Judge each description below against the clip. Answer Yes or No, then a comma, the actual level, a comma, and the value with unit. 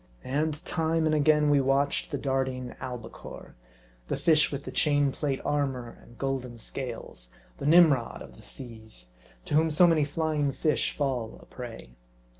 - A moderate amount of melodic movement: Yes, average, 3.3 semitones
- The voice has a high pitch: No, medium, 140 Hz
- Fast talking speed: No, average, 165 wpm